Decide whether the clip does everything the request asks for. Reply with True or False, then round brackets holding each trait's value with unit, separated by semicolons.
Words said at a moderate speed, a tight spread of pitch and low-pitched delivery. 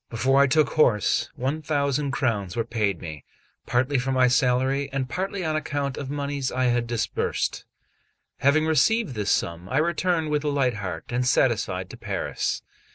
False (170 wpm; 3.6 semitones; 130 Hz)